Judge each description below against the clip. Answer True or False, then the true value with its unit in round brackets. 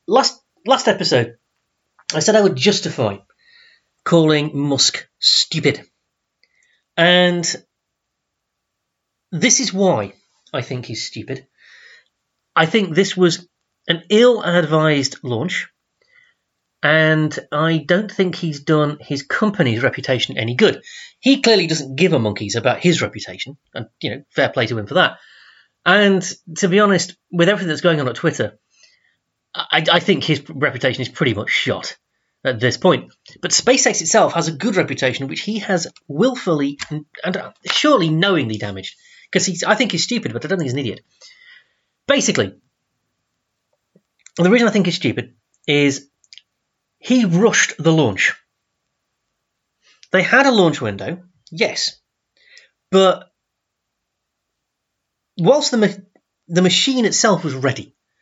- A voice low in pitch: False (175 Hz)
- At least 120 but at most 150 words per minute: True (135 wpm)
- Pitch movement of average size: False (6.5 semitones)